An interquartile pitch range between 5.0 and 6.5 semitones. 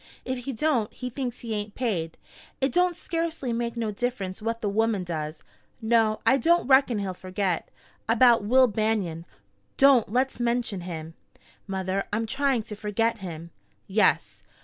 No: average, 4.2 semitones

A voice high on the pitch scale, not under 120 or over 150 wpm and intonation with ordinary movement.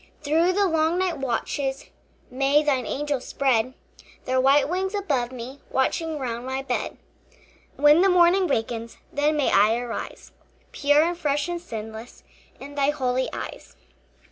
Yes: very high, 280 Hz; average, 145 wpm; average, 3.9 semitones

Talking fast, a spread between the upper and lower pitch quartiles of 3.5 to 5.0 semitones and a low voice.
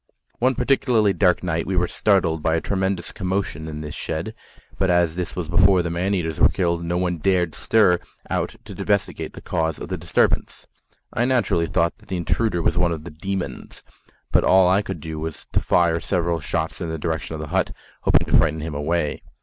No: fast, 210 wpm; average, 2.8 semitones; very low, 85 Hz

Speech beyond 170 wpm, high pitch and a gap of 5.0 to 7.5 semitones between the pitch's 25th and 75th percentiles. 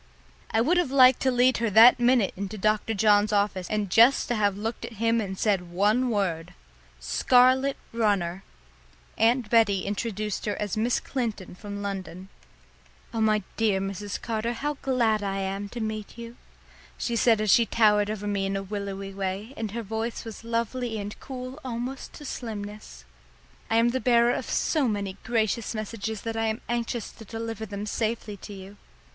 No: average, 180 wpm; high, 220 Hz; narrow, 2.6 semitones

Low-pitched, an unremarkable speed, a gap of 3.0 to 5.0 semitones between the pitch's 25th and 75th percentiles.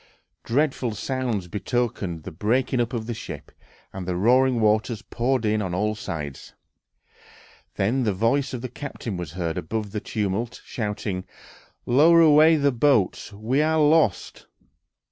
Yes: low, 115 Hz; average, 145 wpm; average, 4.7 semitones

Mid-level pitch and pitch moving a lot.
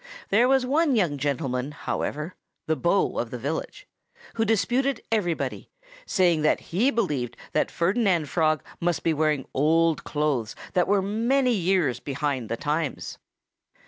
Yes: medium, 170 Hz; wide, 6.6 semitones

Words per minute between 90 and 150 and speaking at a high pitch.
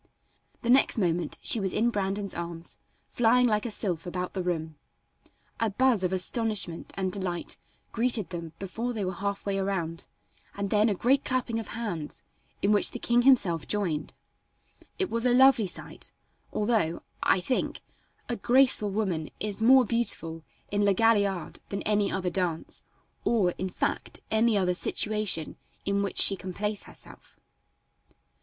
No: average, 160 wpm; high, 200 Hz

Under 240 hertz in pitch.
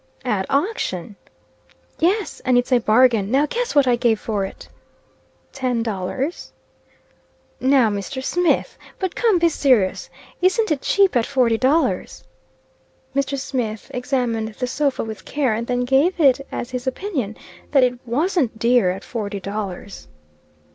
No: very high, 250 Hz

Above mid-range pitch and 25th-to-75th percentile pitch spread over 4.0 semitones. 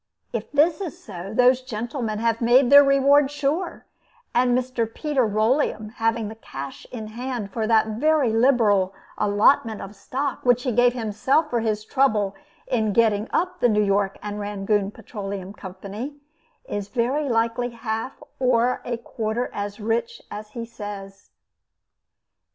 No: high, 230 Hz; average, 3.3 semitones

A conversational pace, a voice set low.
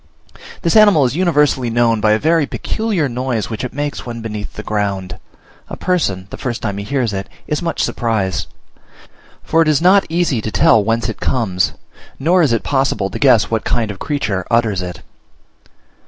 Yes: average, 185 wpm; low, 120 Hz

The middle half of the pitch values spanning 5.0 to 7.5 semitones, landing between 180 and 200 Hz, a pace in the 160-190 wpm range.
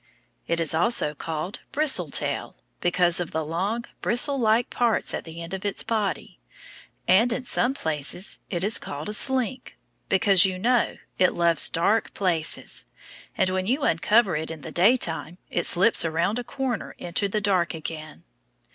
Yes: wide, 5.5 semitones; medium, 185 Hz; average, 165 wpm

